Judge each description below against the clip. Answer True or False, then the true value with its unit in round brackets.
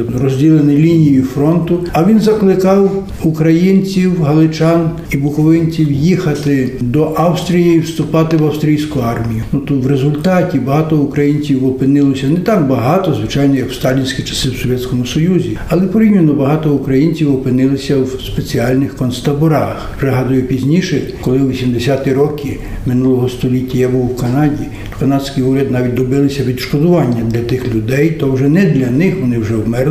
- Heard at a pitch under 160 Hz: True (140 Hz)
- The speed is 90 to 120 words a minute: False (145 wpm)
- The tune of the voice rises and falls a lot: False (3.7 semitones)